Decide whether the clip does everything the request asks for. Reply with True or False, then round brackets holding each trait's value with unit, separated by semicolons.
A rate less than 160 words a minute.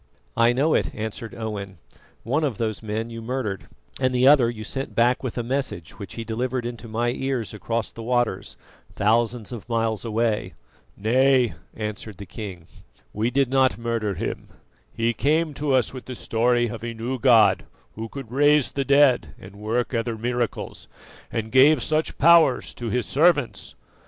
False (170 wpm)